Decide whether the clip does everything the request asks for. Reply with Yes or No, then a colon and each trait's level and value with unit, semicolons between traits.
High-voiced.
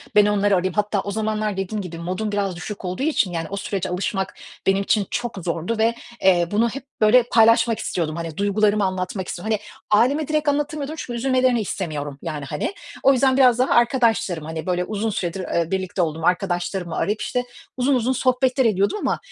Yes: high, 205 Hz